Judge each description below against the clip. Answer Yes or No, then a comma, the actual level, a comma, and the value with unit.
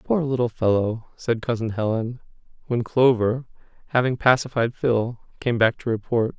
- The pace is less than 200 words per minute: Yes, average, 140 wpm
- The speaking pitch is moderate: No, low, 120 Hz